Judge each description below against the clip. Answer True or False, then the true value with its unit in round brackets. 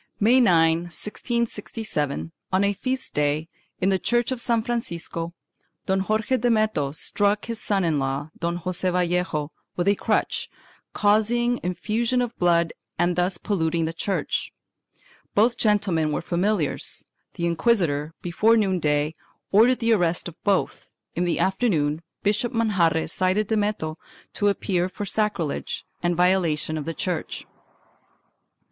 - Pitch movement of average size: True (4.5 semitones)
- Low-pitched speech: False (185 Hz)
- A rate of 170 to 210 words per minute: False (140 wpm)